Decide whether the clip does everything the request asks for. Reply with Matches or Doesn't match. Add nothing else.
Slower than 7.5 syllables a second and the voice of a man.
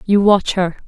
Doesn't match